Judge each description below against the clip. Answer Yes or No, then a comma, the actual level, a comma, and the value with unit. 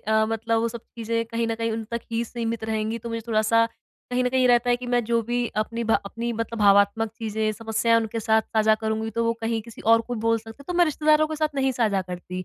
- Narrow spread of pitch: Yes, narrow, 1.2 semitones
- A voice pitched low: No, high, 230 Hz